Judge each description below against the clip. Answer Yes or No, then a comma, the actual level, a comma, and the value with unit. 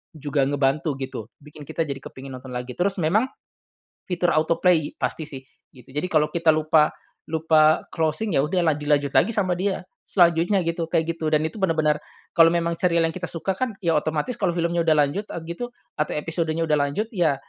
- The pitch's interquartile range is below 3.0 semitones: Yes, narrow, 2.5 semitones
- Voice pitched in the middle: Yes, medium, 160 Hz